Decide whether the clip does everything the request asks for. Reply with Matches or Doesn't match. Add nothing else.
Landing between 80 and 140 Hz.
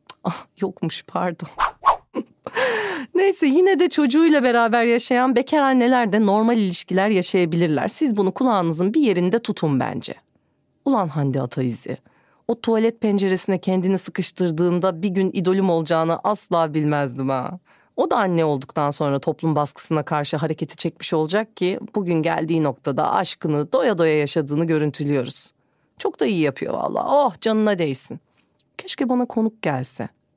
Doesn't match